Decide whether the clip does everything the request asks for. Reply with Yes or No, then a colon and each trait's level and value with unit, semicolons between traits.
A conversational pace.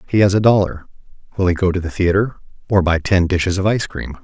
No: fast, 240 wpm